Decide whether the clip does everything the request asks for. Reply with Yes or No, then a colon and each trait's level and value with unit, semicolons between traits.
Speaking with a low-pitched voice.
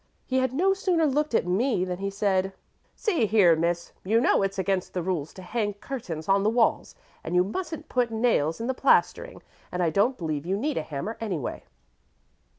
No: high, 200 Hz